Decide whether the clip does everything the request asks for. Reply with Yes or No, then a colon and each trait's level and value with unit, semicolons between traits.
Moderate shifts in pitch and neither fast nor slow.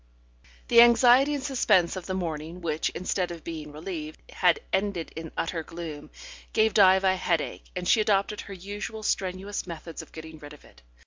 Yes: average, 4.0 semitones; average, 180 wpm